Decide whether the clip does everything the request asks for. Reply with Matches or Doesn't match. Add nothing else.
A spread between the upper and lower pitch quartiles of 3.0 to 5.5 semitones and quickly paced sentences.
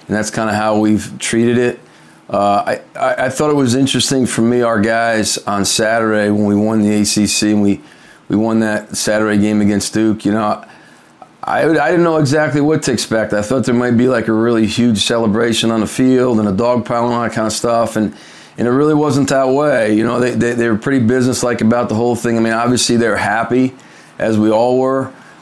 Doesn't match